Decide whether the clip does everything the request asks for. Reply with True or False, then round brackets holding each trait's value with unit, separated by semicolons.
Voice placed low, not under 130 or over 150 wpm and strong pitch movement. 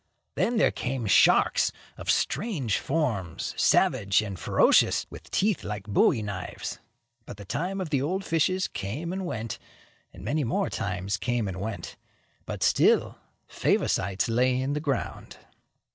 True (120 Hz; 145 wpm; 8.2 semitones)